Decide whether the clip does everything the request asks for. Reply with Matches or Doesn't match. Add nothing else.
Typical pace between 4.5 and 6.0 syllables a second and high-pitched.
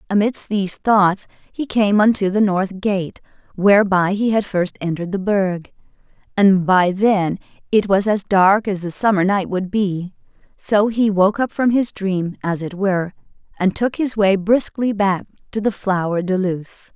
Doesn't match